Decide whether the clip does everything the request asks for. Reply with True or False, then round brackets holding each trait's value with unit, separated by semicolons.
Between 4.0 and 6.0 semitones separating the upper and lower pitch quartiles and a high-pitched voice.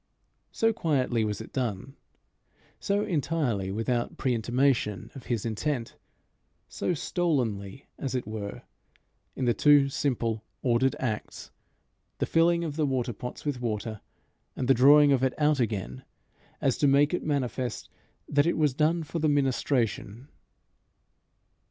False (4.3 semitones; 130 Hz)